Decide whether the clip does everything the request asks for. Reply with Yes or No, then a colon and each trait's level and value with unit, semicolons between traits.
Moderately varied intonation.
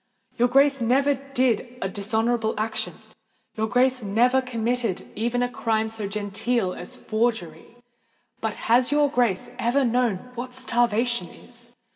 No: narrow, 2.3 semitones